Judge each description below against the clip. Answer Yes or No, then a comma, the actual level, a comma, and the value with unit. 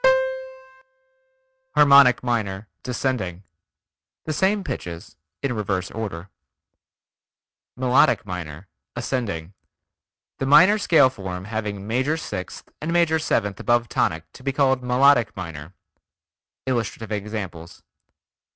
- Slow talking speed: Yes, slow, 95 wpm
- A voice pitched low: Yes, low, 115 Hz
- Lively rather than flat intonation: Yes, wide, 5.9 semitones